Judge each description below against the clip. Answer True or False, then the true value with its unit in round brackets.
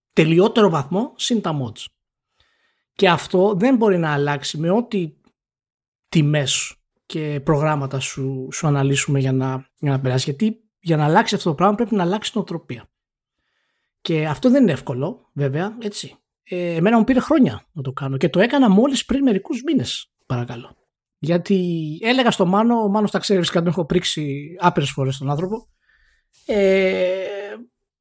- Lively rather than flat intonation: True (6.5 semitones)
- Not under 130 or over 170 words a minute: True (160 wpm)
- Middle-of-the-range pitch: True (175 Hz)